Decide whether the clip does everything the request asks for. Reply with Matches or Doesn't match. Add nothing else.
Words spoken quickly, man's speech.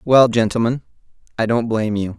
Doesn't match